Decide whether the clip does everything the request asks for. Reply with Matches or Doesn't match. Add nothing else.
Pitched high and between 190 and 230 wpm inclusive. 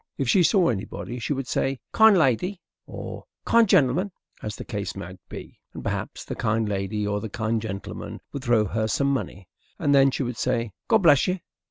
Doesn't match